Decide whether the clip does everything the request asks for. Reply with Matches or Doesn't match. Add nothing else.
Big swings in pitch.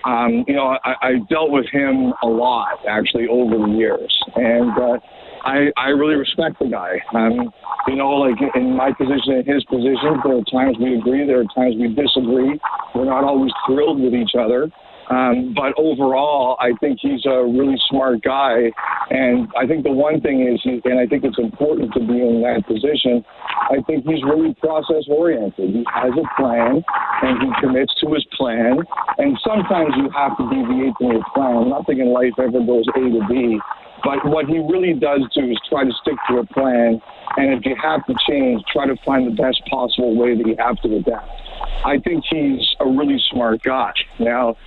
Doesn't match